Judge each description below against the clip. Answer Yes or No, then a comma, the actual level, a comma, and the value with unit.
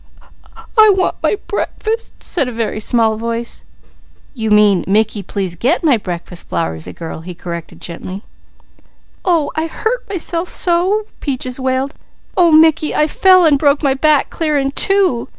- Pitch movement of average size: No, wide, 8.1 semitones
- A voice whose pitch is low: No, very high, 270 Hz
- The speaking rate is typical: Yes, average, 150 wpm